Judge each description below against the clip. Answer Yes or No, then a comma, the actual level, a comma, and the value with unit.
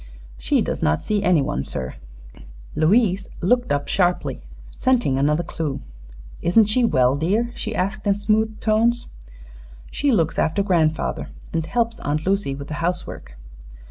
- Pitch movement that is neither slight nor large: No, wide, 6.3 semitones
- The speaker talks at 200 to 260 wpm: No, average, 140 wpm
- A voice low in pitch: No, medium, 180 Hz